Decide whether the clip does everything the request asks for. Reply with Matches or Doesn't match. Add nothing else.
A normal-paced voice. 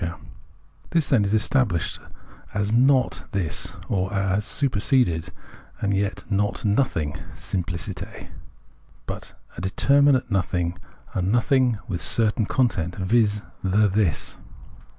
Doesn't match